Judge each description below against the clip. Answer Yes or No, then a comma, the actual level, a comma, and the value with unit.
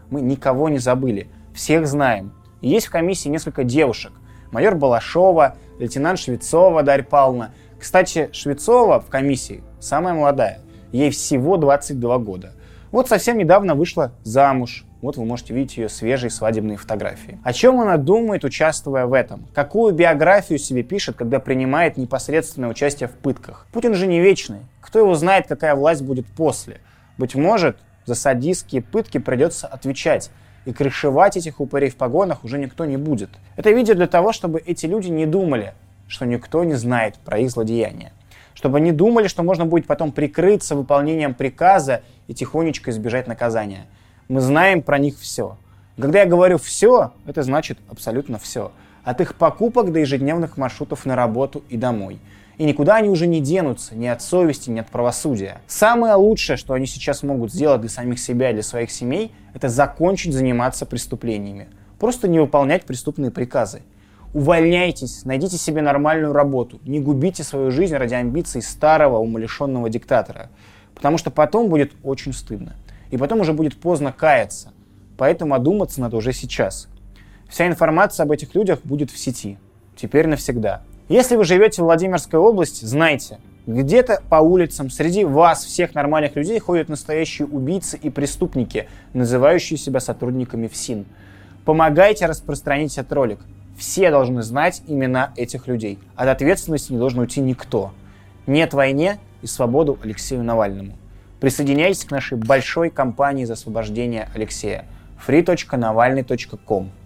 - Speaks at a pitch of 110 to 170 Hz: Yes, low, 135 Hz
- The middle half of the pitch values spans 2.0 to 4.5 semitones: No, wide, 5.4 semitones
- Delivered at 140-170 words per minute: Yes, average, 150 wpm